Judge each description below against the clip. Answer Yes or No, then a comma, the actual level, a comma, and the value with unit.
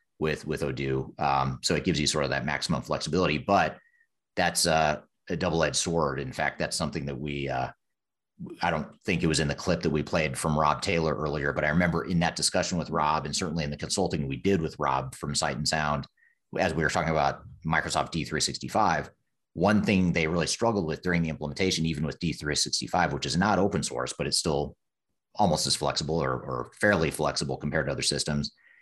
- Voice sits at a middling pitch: No, very low, 80 Hz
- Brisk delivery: Yes, fast, 210 wpm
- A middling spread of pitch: Yes, average, 3.0 semitones